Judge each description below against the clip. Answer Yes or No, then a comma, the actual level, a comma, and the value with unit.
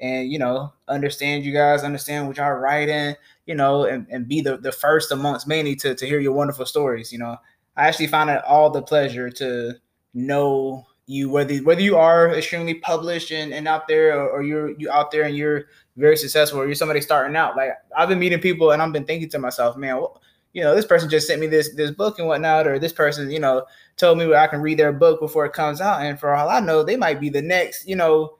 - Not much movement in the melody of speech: Yes, narrow, 1.9 semitones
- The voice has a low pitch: No, medium, 150 Hz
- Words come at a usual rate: No, fast, 245 wpm